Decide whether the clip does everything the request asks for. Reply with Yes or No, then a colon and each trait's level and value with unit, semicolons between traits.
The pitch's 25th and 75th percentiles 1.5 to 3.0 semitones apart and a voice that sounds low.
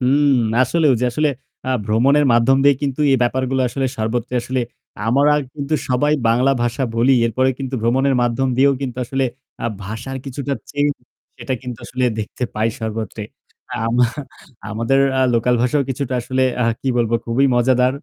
Yes: narrow, 2.6 semitones; low, 130 Hz